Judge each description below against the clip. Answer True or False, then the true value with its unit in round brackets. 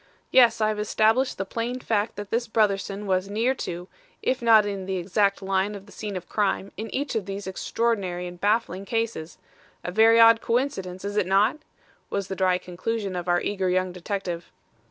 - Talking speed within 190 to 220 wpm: True (195 wpm)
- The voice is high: True (200 Hz)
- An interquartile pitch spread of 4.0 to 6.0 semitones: False (3.3 semitones)